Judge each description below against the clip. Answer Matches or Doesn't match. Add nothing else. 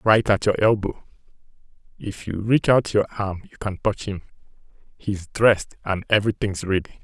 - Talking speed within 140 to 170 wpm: Matches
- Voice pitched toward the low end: Matches